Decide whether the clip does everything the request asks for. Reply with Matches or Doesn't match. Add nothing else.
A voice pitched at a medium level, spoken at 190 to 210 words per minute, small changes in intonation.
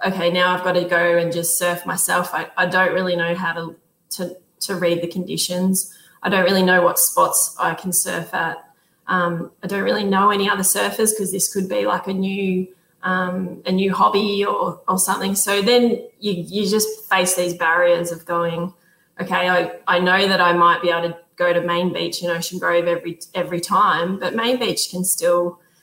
Matches